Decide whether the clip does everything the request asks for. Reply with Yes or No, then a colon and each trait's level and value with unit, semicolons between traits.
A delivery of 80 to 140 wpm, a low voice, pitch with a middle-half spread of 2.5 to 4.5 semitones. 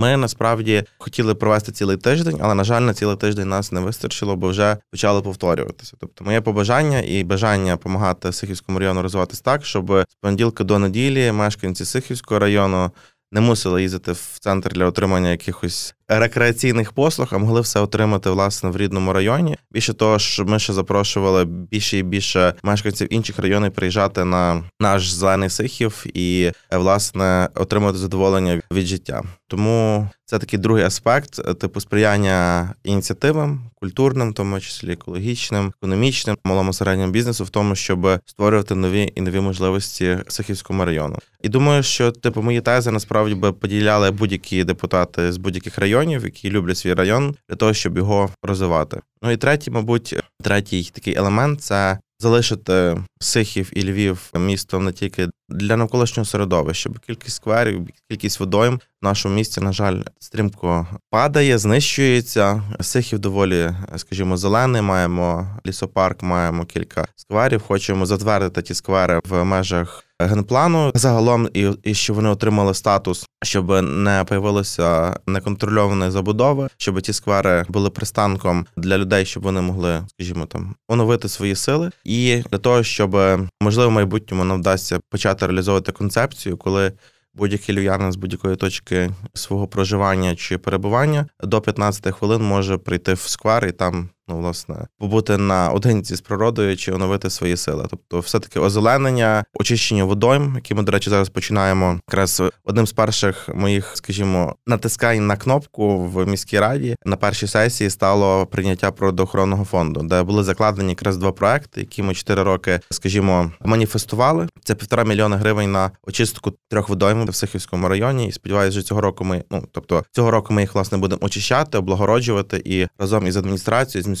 No: fast, 155 wpm; low, 100 Hz; average, 2.8 semitones